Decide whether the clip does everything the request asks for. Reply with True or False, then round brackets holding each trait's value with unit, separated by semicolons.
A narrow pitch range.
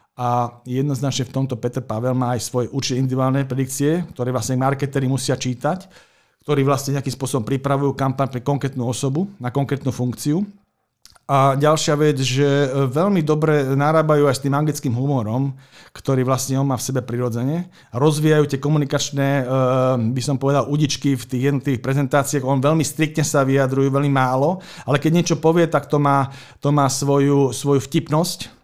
True (2.0 semitones)